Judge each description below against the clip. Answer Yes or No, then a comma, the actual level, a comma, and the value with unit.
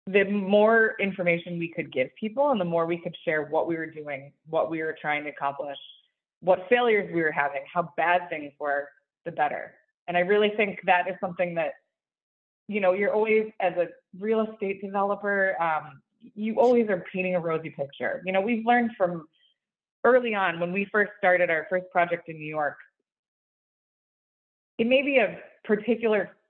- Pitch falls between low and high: Yes, medium, 180 Hz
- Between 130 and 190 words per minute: Yes, average, 185 wpm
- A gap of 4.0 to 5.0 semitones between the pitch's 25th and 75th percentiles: Yes, average, 4.5 semitones